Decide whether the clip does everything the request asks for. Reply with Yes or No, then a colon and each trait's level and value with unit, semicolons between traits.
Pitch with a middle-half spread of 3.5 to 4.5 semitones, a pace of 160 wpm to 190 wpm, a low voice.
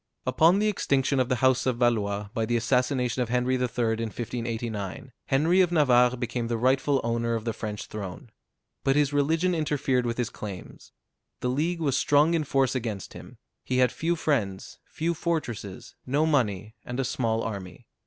Yes: average, 4.0 semitones; average, 180 wpm; low, 125 Hz